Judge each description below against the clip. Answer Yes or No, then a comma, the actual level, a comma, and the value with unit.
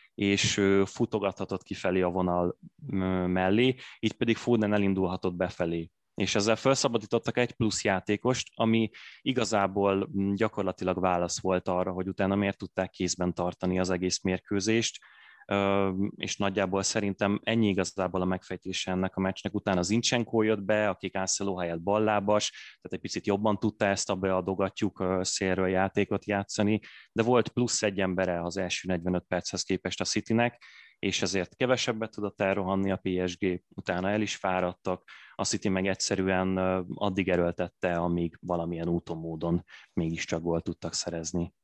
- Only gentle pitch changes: Yes, narrow, 2.3 semitones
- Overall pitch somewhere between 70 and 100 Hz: Yes, very low, 95 Hz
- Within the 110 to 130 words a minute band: No, average, 140 wpm